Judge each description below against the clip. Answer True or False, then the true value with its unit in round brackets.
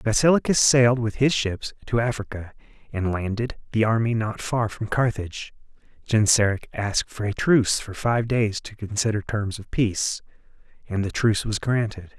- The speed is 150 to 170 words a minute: True (165 wpm)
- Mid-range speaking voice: False (110 Hz)